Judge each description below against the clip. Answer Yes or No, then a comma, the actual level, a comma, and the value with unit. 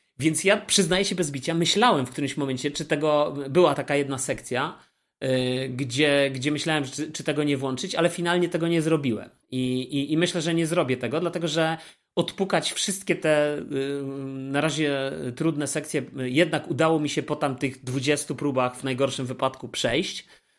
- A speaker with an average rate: No, fast, 180 wpm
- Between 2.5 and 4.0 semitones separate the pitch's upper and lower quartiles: Yes, average, 3.4 semitones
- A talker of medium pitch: Yes, medium, 150 Hz